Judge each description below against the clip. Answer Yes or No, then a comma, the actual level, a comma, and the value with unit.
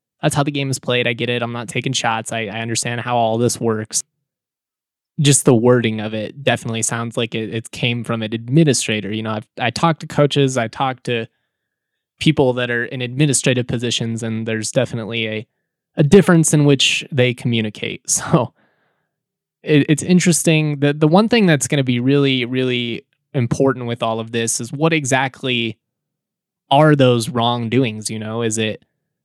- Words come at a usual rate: Yes, average, 185 wpm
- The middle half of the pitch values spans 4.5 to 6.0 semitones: No, average, 4.0 semitones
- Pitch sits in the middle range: No, low, 125 Hz